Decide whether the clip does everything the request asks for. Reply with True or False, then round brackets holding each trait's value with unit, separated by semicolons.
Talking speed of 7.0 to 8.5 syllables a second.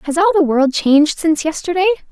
True (7.2 syllables/s)